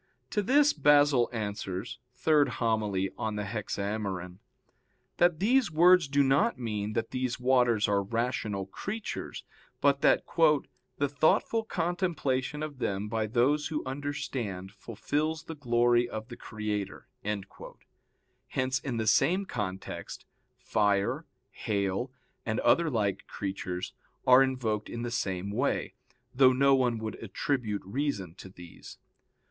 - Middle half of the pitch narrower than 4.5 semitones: No, wide, 5.6 semitones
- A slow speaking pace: Yes, slow, 125 wpm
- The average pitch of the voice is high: No, low, 120 Hz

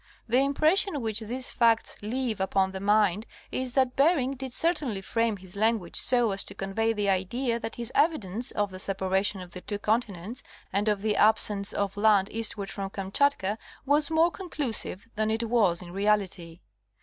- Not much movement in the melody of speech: No, average, 4.2 semitones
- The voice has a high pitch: Yes, high, 215 Hz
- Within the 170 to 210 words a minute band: Yes, average, 180 wpm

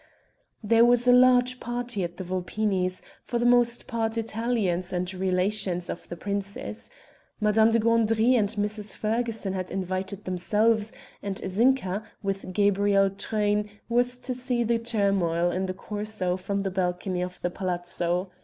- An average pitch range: Yes, average, 3.7 semitones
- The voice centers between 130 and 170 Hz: No, high, 205 Hz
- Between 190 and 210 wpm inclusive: No, average, 150 wpm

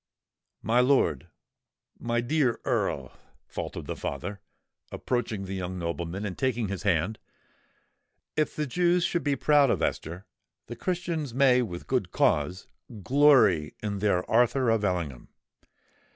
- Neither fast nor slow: No, slow, 130 wpm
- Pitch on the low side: Yes, low, 115 Hz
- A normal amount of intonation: No, wide, 6.8 semitones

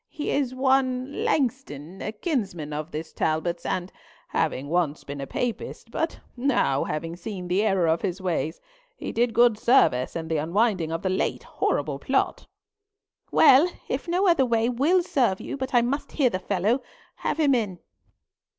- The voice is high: Yes, high, 215 Hz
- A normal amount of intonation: No, wide, 7.6 semitones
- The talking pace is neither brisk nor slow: Yes, average, 170 wpm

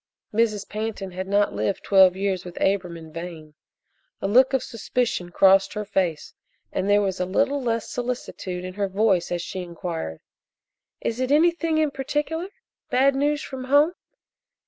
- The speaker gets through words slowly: No, average, 165 wpm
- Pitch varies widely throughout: Yes, wide, 5.9 semitones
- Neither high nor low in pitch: No, high, 205 Hz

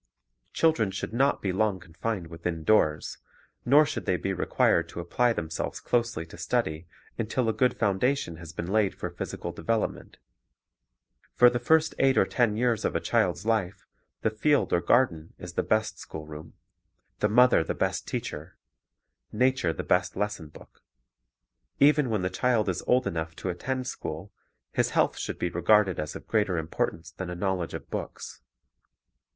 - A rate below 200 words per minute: Yes, average, 170 wpm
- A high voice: No, low, 100 Hz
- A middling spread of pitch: No, wide, 6.1 semitones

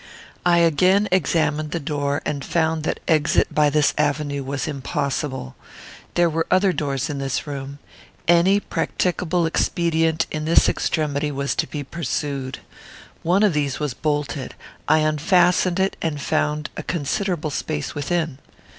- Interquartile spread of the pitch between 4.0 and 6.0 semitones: No, average, 3.0 semitones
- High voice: No, medium, 155 Hz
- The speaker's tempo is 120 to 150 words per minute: Yes, average, 145 wpm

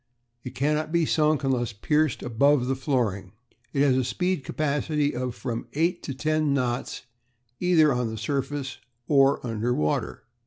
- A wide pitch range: No, average, 3.7 semitones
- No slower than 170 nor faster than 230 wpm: No, average, 155 wpm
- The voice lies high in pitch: No, low, 135 Hz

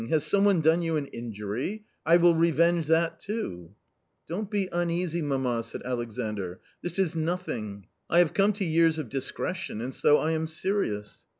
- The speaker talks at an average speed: Yes, average, 180 wpm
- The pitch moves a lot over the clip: Yes, wide, 6.0 semitones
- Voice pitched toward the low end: No, medium, 160 Hz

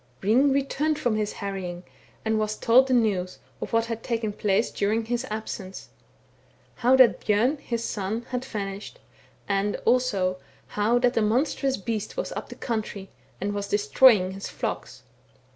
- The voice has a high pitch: Yes, high, 220 Hz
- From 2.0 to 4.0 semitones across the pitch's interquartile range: Yes, average, 3.6 semitones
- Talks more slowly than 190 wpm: Yes, average, 165 wpm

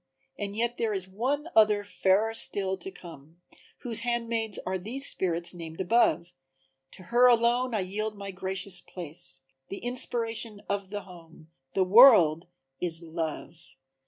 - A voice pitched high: Yes, high, 200 Hz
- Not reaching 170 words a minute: Yes, average, 145 wpm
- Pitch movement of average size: Yes, average, 4.7 semitones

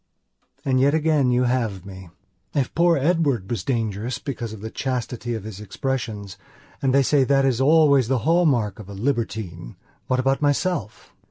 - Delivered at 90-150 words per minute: No, average, 165 wpm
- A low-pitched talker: Yes, low, 125 Hz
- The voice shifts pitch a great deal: No, average, 4.4 semitones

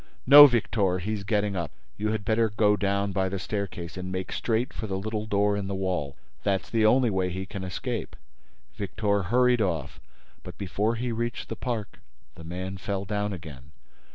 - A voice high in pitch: No, low, 100 Hz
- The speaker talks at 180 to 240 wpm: Yes, average, 185 wpm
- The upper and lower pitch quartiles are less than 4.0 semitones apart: Yes, average, 2.8 semitones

